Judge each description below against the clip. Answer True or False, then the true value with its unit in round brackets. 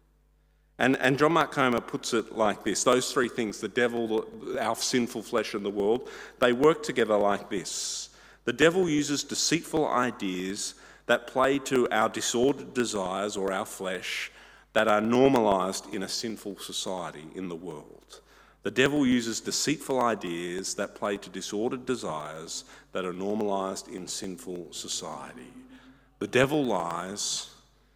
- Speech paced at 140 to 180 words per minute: True (150 wpm)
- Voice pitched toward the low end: True (115 Hz)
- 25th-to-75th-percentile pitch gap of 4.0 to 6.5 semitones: True (5.2 semitones)